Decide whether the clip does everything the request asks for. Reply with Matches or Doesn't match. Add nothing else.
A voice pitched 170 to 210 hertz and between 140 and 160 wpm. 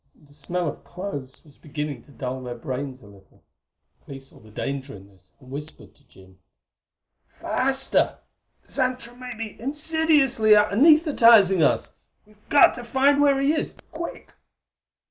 Matches